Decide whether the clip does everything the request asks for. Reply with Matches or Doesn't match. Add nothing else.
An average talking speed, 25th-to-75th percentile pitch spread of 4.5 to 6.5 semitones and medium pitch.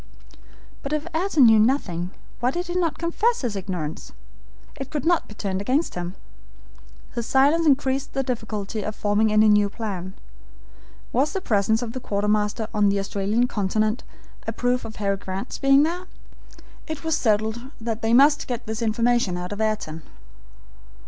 Doesn't match